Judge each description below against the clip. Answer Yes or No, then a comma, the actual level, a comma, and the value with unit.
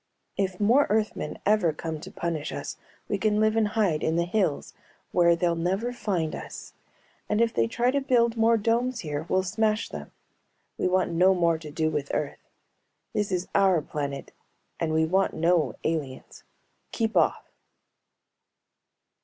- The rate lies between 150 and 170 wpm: Yes, average, 160 wpm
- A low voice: No, medium, 185 Hz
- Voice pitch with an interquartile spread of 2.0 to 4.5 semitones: No, average, 5.1 semitones